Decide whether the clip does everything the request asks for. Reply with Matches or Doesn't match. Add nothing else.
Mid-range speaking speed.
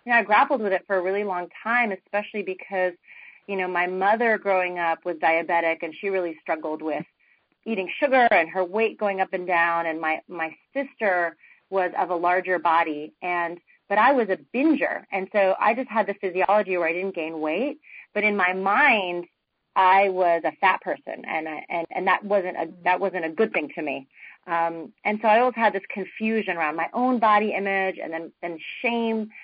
Doesn't match